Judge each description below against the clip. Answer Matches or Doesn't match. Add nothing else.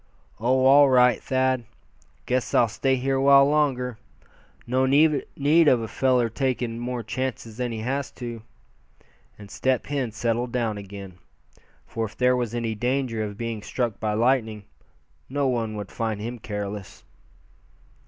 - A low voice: Matches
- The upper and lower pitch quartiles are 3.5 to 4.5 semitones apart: Doesn't match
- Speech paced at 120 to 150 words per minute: Matches